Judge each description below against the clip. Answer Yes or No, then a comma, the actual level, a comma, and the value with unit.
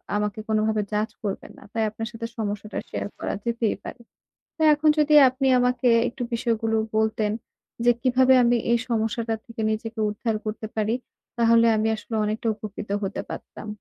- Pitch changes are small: Yes, narrow, 1.8 semitones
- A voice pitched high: Yes, high, 225 Hz